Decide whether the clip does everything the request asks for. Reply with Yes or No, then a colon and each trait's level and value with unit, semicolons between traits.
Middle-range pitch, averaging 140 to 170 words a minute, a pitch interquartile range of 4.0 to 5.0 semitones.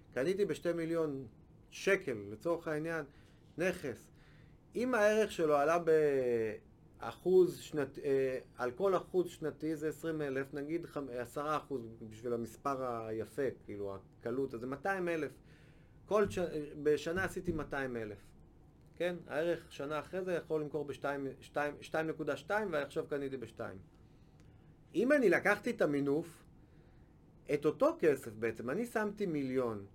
No: medium, 150 Hz; average, 125 wpm; average, 4.5 semitones